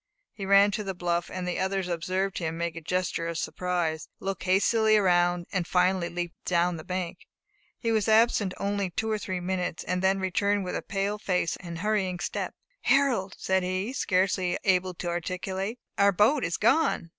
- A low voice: No, medium, 185 Hz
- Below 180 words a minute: No, average, 185 wpm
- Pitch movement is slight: Yes, narrow, 2.2 semitones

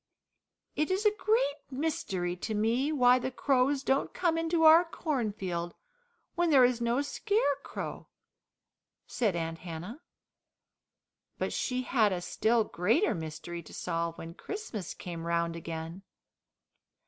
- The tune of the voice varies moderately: No, wide, 8.9 semitones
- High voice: Yes, high, 235 Hz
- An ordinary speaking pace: No, slow, 130 wpm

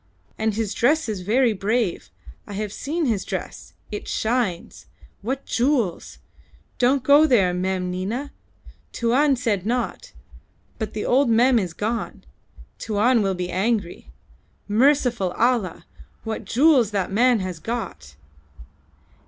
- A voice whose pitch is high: Yes, high, 225 Hz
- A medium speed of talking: No, slow, 130 wpm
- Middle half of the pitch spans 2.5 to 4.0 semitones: No, average, 4.5 semitones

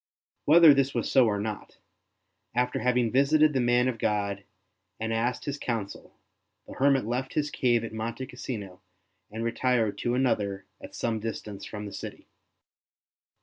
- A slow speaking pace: No, average, 155 wpm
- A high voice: No, low, 120 Hz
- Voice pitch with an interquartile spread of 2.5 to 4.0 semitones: Yes, average, 3.4 semitones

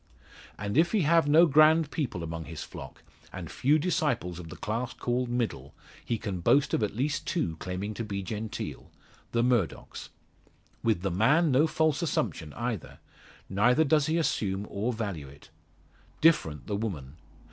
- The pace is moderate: Yes, average, 165 wpm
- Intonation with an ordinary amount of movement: No, wide, 7.9 semitones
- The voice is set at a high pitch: No, low, 115 Hz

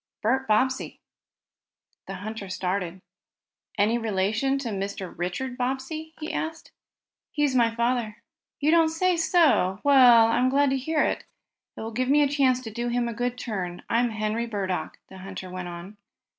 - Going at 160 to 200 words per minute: Yes, average, 165 wpm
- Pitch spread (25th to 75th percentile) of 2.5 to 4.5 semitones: No, average, 5.0 semitones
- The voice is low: No, high, 235 Hz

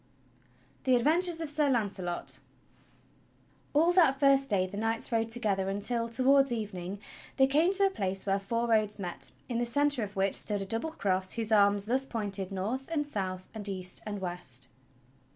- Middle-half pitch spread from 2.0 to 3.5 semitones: No, wide, 5.6 semitones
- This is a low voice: No, high, 225 Hz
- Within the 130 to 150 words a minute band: No, average, 180 wpm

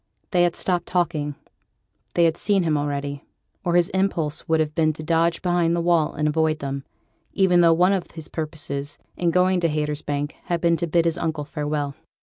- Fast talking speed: No, average, 195 wpm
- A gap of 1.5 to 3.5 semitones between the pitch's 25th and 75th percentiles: Yes, narrow, 2.6 semitones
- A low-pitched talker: No, medium, 165 Hz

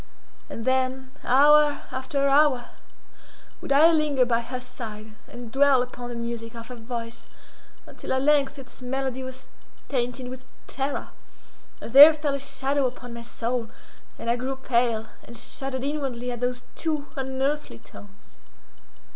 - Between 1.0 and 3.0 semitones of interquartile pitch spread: Yes, narrow, 2.6 semitones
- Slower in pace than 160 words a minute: Yes, average, 150 wpm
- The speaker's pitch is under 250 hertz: No, very high, 260 Hz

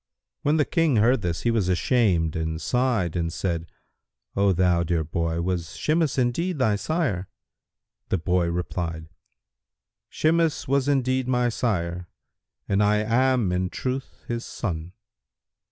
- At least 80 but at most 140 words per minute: Yes, slow, 135 wpm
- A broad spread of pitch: Yes, wide, 7.1 semitones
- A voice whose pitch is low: Yes, low, 100 Hz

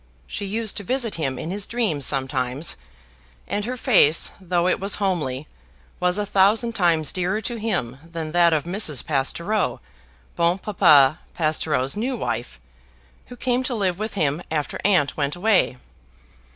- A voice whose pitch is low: No, medium, 180 Hz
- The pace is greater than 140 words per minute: Yes, average, 155 wpm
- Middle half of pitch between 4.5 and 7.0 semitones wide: Yes, wide, 5.6 semitones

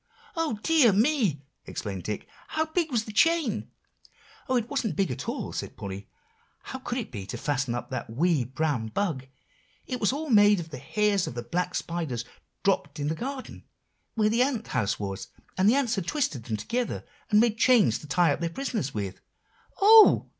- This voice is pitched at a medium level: No, high, 195 Hz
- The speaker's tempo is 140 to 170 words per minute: No, average, 195 wpm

